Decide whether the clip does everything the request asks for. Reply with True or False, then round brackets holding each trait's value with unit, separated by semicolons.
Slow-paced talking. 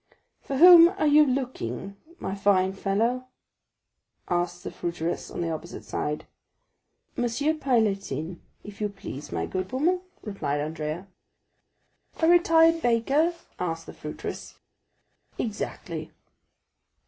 True (110 wpm)